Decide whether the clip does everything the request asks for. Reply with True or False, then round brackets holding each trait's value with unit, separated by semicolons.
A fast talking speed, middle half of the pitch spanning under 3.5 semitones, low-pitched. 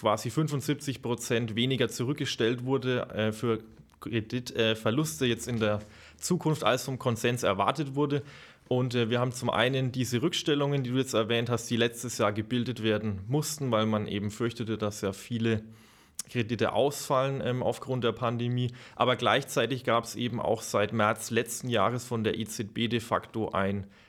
False (165 wpm; 2.7 semitones; 120 Hz)